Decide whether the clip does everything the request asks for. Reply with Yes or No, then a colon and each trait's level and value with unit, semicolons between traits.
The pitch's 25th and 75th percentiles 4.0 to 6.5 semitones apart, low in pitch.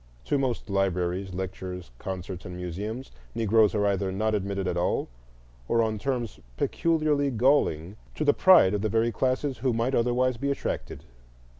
Yes: average, 5.2 semitones; low, 110 Hz